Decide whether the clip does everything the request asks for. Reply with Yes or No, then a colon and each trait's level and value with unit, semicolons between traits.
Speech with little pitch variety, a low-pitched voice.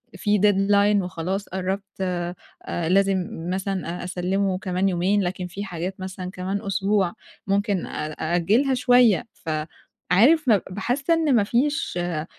No: narrow, 2.3 semitones; high, 195 Hz